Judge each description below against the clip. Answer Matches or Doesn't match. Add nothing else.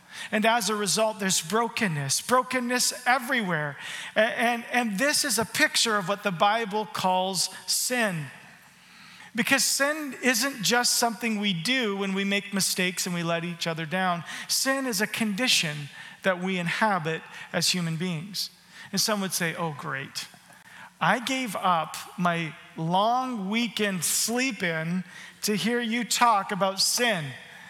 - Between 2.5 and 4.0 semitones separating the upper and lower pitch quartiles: Doesn't match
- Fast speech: Doesn't match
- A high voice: Matches